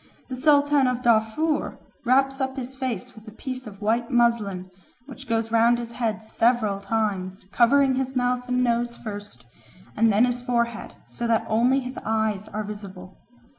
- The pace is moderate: Yes, average, 170 wpm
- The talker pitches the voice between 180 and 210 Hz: No, high, 235 Hz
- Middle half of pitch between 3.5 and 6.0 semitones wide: No, average, 2.8 semitones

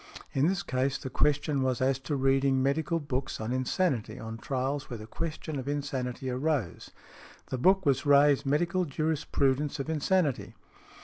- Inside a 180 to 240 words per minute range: No, average, 160 wpm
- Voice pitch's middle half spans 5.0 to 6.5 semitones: No, narrow, 2.5 semitones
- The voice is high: No, medium, 140 Hz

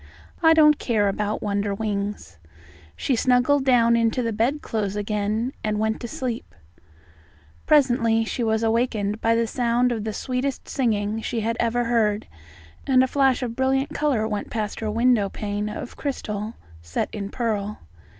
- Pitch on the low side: No, high, 225 Hz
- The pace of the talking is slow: No, average, 155 wpm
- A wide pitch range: No, average, 3.0 semitones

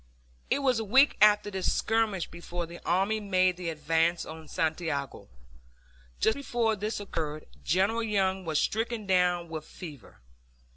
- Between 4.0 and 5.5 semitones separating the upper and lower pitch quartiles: Yes, average, 4.5 semitones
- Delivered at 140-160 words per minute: Yes, average, 145 wpm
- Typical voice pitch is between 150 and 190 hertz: Yes, medium, 185 Hz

